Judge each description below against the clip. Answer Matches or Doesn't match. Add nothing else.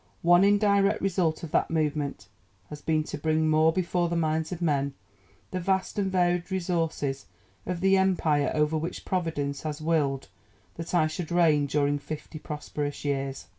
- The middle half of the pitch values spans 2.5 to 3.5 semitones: Matches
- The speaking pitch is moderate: Matches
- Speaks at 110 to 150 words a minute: Doesn't match